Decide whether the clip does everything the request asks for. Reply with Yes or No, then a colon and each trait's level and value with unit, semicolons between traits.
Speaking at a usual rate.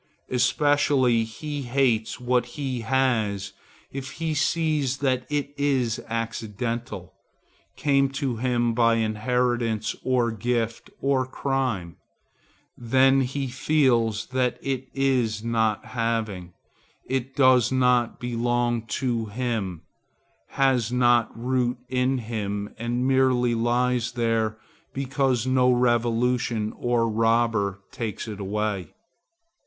No: slow, 105 wpm